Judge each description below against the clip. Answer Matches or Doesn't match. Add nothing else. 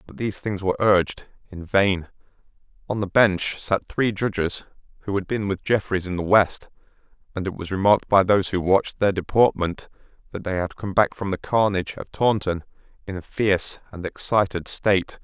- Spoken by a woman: Doesn't match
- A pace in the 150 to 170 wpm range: Doesn't match